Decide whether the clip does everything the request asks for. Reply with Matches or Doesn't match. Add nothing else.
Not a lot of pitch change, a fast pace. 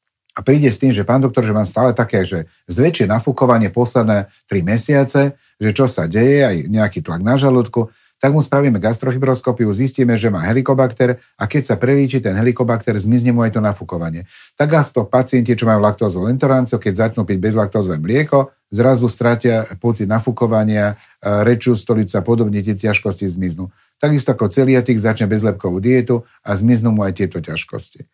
Doesn't match